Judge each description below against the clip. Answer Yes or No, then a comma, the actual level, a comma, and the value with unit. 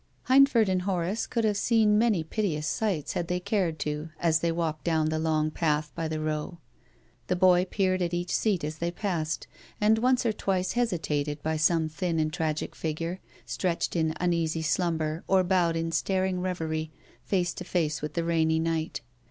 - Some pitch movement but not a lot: Yes, average, 3.0 semitones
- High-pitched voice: No, medium, 170 Hz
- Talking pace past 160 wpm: Yes, average, 185 wpm